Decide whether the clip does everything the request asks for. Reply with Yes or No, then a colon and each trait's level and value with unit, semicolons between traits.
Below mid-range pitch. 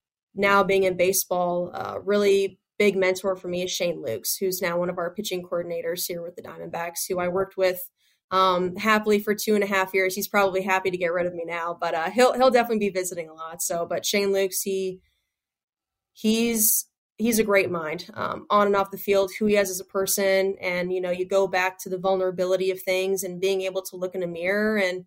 No: high, 190 Hz